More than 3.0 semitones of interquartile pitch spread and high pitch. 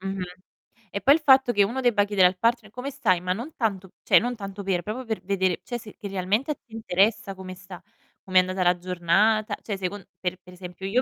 Yes: average, 3.5 semitones; high, 195 Hz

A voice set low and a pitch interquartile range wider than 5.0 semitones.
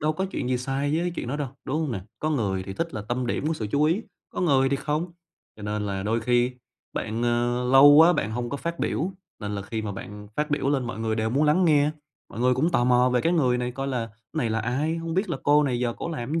No: low, 130 Hz; average, 4.6 semitones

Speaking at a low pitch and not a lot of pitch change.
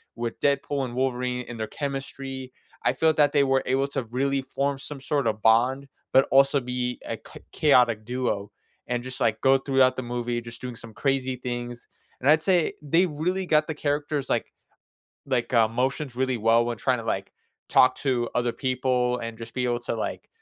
Yes: low, 130 Hz; narrow, 2.3 semitones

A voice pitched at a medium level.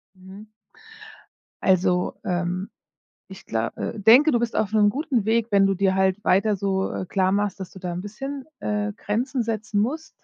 No: high, 205 Hz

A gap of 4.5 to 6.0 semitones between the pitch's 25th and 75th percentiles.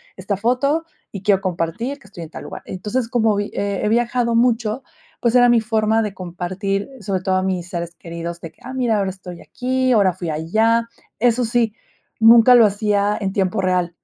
No: average, 3.9 semitones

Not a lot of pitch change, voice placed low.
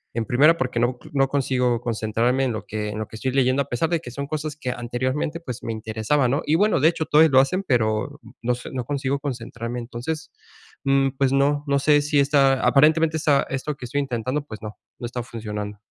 No: average, 3.4 semitones; low, 130 Hz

